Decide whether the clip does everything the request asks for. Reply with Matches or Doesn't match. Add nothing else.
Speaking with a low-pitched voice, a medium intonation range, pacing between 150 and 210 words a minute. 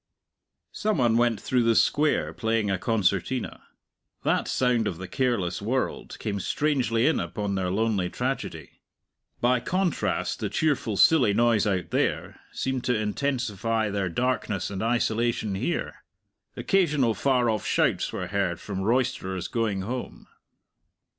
Doesn't match